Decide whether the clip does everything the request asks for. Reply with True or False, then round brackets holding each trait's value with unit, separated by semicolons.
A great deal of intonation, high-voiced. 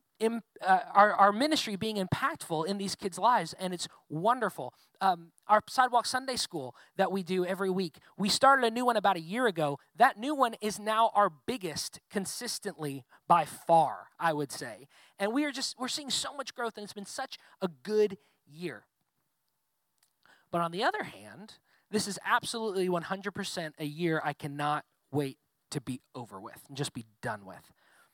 True (6.1 semitones; 195 Hz)